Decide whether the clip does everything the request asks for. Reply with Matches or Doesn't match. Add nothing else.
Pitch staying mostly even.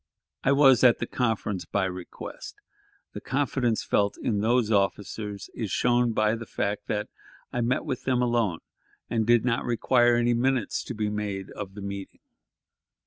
Doesn't match